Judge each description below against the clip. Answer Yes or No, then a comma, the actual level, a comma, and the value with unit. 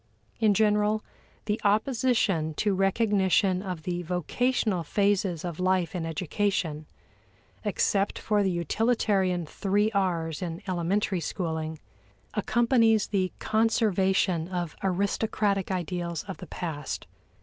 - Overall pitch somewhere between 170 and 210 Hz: Yes, high, 190 Hz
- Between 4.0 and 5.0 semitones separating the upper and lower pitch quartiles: No, average, 3.2 semitones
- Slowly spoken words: Yes, slow, 110 wpm